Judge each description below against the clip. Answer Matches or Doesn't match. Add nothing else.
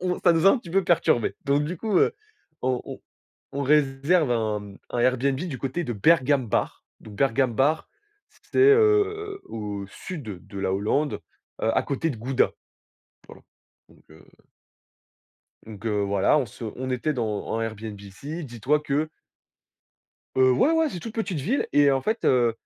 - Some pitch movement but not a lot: Doesn't match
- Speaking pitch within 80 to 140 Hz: Matches